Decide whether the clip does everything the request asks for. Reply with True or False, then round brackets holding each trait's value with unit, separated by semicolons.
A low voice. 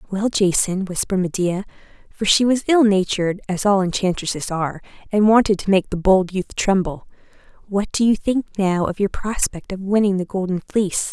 False (195 Hz)